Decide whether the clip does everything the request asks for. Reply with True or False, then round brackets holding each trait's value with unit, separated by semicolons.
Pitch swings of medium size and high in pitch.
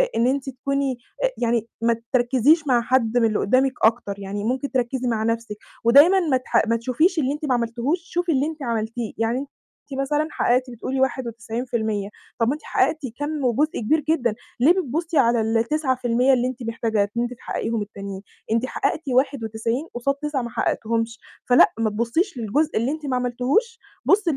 True (3.6 semitones; 250 Hz)